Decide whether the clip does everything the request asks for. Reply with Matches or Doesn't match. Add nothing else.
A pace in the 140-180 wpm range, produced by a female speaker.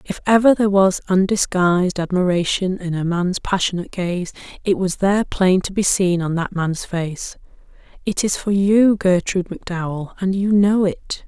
Matches